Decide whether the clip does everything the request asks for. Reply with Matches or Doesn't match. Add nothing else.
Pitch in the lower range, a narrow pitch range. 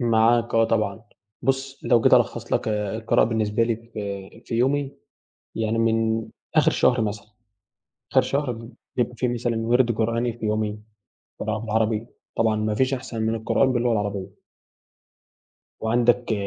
Matches